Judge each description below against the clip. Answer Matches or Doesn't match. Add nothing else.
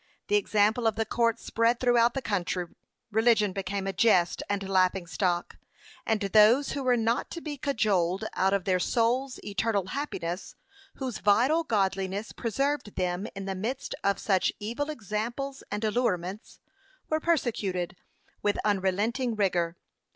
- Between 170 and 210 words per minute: Doesn't match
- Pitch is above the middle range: Matches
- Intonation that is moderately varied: Matches